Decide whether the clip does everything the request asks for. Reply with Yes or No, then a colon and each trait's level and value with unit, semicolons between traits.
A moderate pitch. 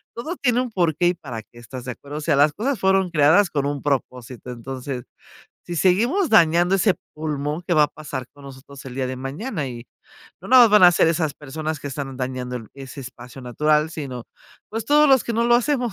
Yes: medium, 150 Hz